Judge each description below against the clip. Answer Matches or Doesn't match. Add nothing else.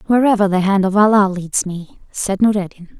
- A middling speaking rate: Matches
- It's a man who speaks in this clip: Doesn't match